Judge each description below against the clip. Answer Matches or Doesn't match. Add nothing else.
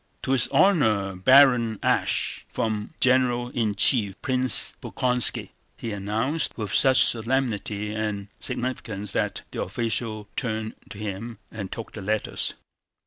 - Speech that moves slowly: Matches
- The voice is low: Matches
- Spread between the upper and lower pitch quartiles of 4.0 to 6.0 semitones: Doesn't match